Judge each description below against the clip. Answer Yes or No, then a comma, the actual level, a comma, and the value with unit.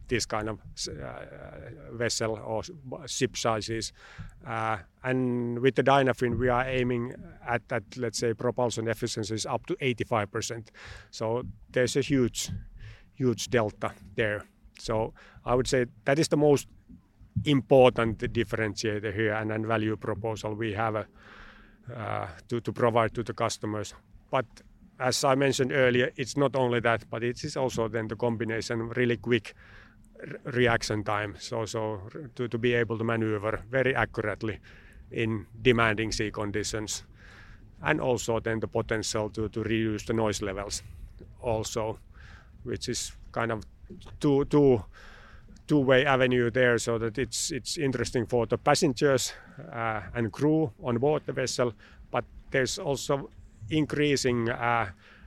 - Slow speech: No, average, 145 wpm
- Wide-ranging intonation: No, narrow, 2.6 semitones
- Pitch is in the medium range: No, low, 115 Hz